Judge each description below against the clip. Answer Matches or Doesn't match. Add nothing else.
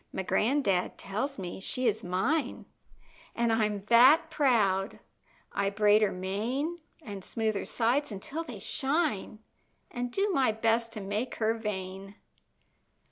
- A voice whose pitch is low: Doesn't match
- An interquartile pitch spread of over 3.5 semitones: Matches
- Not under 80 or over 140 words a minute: Matches